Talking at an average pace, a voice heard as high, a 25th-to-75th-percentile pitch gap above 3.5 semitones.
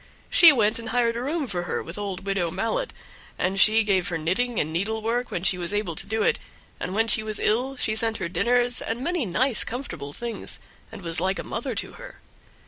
No: fast, 220 wpm; high, 215 Hz; average, 4.6 semitones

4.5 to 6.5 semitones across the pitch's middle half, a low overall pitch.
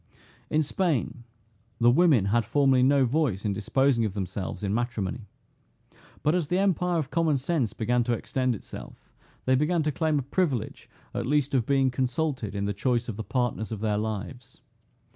Yes: average, 5.0 semitones; low, 125 Hz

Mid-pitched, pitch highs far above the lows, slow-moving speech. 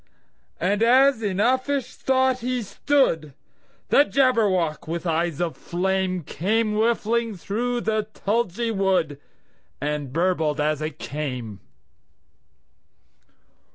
No: high, 195 Hz; wide, 6.7 semitones; slow, 90 wpm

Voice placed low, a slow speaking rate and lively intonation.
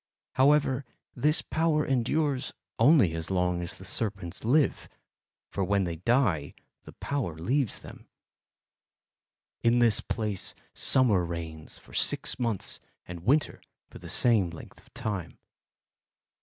Yes: low, 110 Hz; slow, 130 wpm; wide, 7.2 semitones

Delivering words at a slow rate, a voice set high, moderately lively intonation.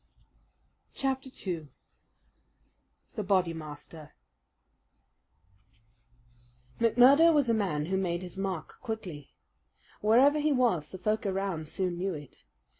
No: slow, 105 wpm; high, 195 Hz; wide, 5.9 semitones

